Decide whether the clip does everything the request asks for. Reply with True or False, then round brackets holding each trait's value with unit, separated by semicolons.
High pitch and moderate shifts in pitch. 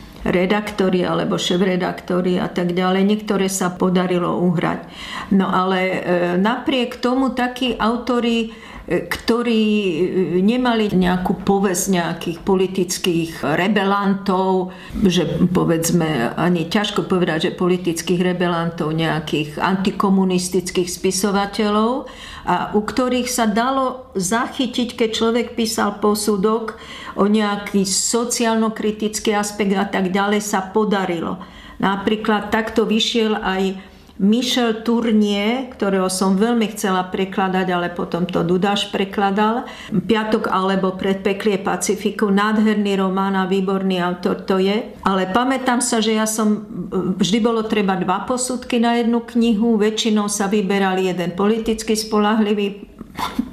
True (205 Hz; 3.1 semitones)